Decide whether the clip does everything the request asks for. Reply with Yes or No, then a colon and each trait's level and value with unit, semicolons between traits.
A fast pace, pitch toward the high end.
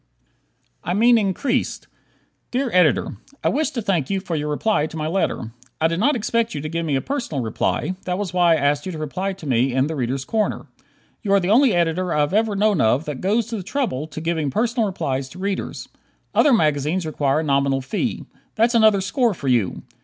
No: fast, 220 wpm; medium, 175 Hz